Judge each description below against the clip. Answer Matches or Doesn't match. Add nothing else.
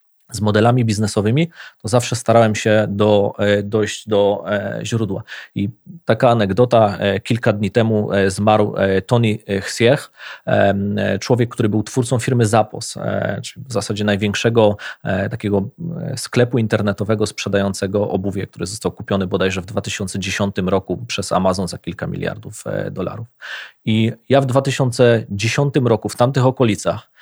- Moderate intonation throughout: Matches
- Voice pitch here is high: Doesn't match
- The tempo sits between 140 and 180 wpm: Doesn't match